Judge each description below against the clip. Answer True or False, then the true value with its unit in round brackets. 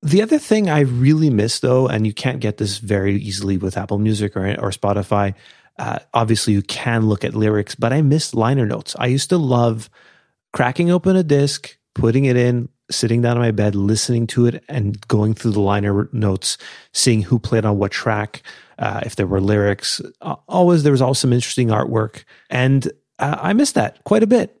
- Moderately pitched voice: False (115 Hz)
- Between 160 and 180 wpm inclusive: False (200 wpm)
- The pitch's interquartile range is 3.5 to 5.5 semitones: True (4.1 semitones)